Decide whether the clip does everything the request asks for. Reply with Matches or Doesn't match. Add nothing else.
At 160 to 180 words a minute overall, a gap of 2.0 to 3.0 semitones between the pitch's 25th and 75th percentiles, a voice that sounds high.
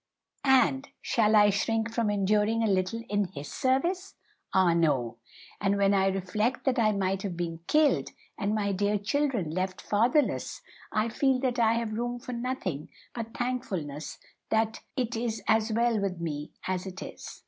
Doesn't match